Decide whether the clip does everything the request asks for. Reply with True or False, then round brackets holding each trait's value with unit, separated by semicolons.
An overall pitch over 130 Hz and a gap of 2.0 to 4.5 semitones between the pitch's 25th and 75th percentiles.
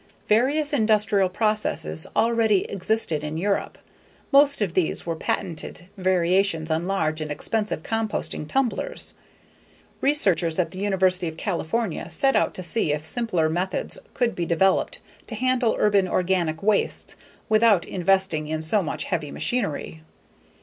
False (190 Hz; 5.0 semitones)